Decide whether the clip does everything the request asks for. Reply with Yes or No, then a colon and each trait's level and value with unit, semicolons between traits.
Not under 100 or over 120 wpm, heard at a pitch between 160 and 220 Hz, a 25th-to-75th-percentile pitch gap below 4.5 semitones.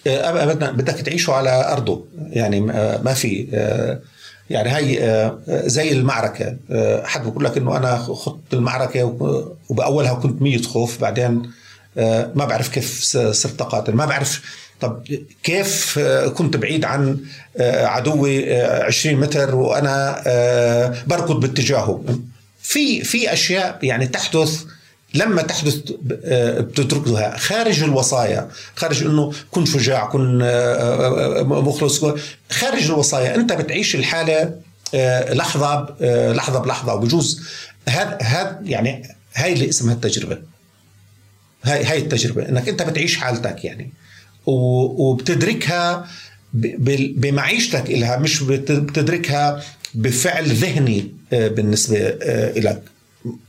No: average, 105 wpm; low, 135 Hz; average, 4.1 semitones